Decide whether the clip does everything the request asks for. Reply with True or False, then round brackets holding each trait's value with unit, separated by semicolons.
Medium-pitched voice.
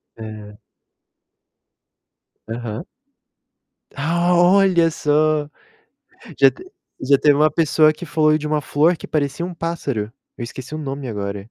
True (150 Hz)